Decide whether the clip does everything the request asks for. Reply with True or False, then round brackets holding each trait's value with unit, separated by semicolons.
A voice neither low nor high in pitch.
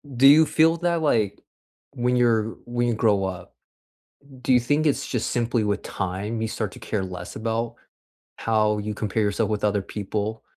False (110 Hz)